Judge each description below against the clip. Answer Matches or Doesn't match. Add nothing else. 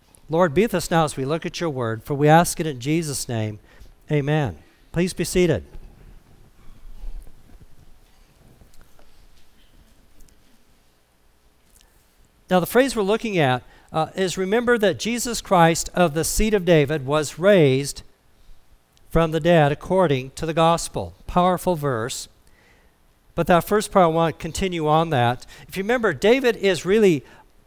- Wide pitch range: Matches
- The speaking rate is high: Doesn't match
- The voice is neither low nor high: Matches